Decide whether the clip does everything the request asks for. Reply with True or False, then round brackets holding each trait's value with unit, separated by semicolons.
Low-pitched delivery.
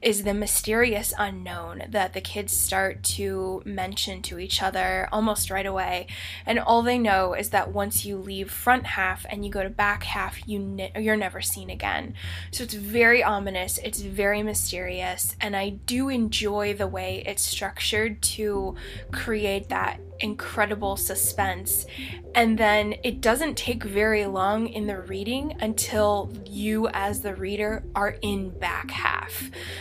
False (195 Hz)